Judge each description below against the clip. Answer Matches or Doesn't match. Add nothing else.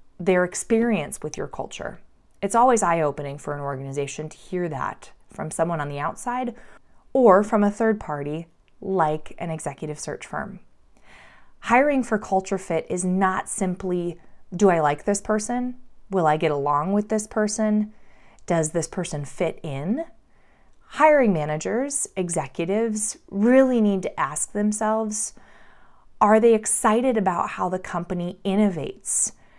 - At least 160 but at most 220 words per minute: Doesn't match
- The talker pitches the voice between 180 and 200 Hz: Matches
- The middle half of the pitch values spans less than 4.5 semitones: Doesn't match